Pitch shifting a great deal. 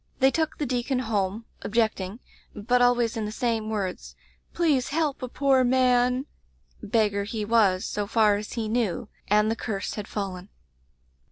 No: average, 3.2 semitones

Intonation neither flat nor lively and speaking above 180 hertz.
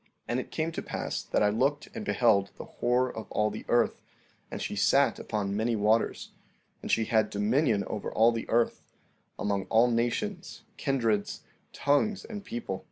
No: average, 4.4 semitones; low, 115 Hz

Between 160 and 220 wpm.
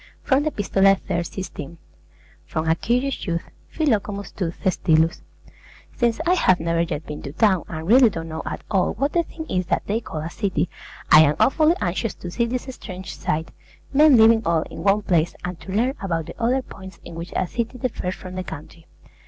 Yes: average, 200 wpm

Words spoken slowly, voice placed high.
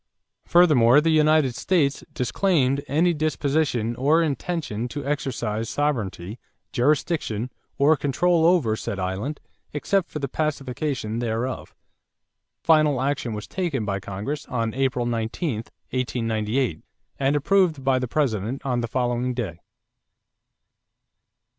No: slow, 115 wpm; low, 135 Hz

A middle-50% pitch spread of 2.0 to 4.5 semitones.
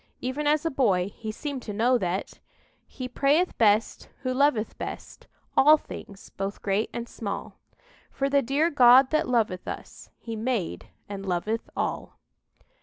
No: average, 5.1 semitones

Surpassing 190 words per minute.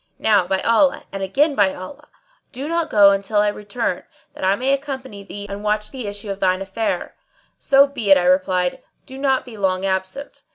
Yes: average, 200 wpm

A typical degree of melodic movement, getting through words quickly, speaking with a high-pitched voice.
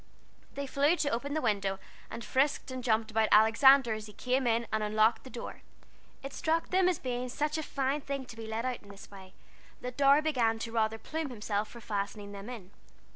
Yes: average, 4.2 semitones; fast, 215 wpm; high, 240 Hz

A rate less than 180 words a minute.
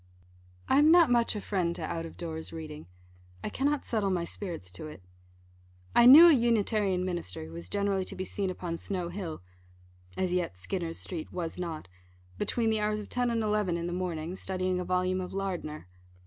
No: average, 195 wpm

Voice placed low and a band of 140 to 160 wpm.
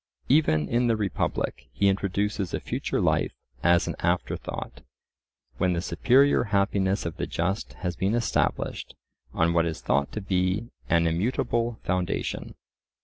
Yes: very low, 95 Hz; average, 145 wpm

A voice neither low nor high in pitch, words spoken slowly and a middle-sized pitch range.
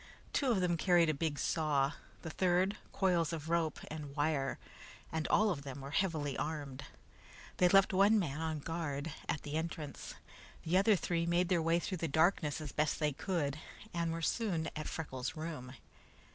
No: medium, 160 Hz; average, 180 wpm; average, 3.1 semitones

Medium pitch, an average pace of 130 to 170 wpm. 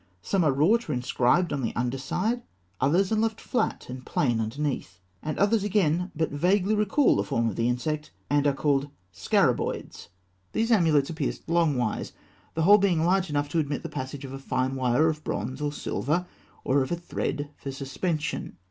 No: medium, 150 Hz; average, 185 wpm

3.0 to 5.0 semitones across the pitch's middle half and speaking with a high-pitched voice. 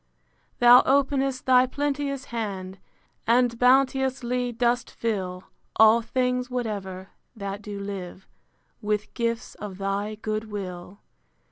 Yes: average, 4.0 semitones; high, 230 Hz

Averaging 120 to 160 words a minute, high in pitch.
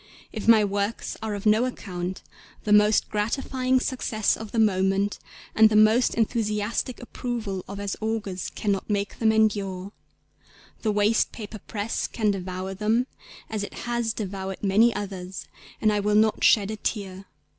Yes: average, 155 wpm; high, 210 Hz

